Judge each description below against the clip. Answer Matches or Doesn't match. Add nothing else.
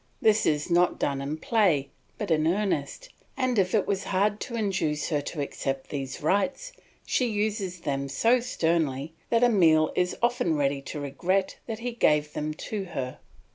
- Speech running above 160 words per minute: Matches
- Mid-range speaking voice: Matches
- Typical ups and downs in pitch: Doesn't match